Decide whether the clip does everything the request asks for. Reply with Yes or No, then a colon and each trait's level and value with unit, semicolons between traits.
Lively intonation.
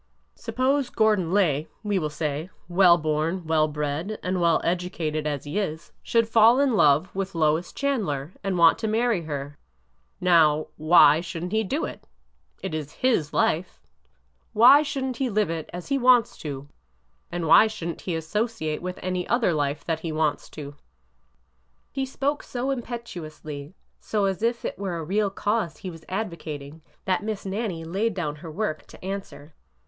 Yes: wide, 5.8 semitones